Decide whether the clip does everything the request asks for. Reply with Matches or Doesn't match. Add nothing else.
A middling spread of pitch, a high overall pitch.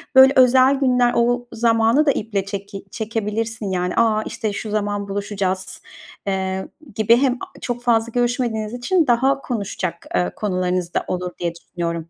Matches